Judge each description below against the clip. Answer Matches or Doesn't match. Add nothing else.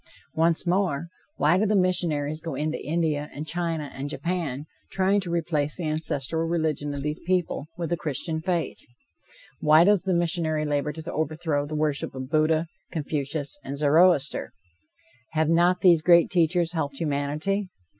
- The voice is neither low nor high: Matches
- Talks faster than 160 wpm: Doesn't match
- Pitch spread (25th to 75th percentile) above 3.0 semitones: Doesn't match